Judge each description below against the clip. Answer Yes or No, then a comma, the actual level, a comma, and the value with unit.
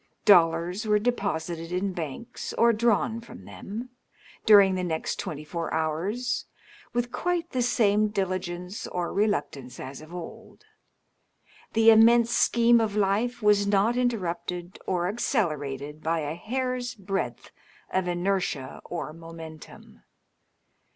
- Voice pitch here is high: Yes, high, 195 Hz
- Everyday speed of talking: No, slow, 125 wpm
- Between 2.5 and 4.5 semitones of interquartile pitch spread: No, average, 5.2 semitones